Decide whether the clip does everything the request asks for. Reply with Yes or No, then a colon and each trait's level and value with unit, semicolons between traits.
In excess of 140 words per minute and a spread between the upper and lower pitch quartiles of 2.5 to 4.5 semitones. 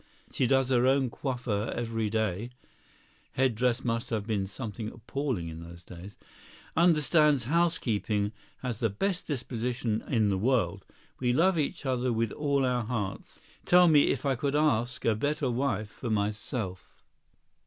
Yes: average, 155 wpm; average, 4.2 semitones